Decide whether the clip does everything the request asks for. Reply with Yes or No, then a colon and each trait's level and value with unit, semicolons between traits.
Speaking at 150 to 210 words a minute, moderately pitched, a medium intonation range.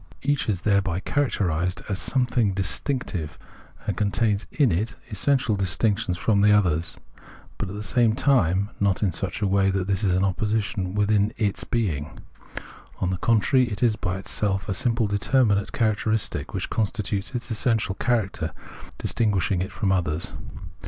No: average, 165 wpm; low, 100 Hz; average, 3.0 semitones